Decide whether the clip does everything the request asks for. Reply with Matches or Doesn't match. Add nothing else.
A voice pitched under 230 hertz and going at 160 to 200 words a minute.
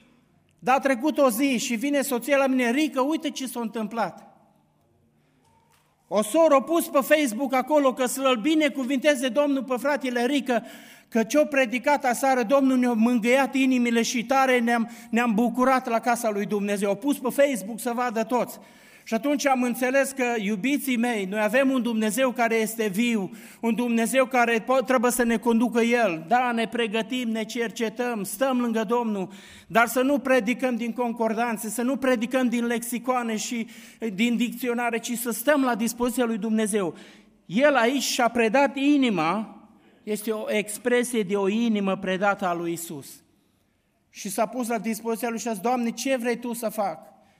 Doesn't match